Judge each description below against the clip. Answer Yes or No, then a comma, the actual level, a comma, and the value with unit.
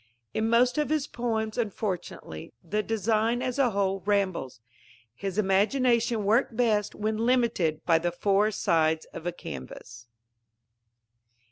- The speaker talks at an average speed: No, slow, 130 wpm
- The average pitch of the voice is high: Yes, high, 210 Hz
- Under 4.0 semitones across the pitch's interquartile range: No, average, 4.4 semitones